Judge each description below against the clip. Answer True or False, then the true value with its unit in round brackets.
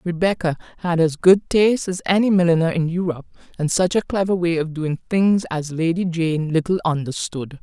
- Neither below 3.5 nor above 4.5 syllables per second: False (5.3 syllables/s)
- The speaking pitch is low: False (170 Hz)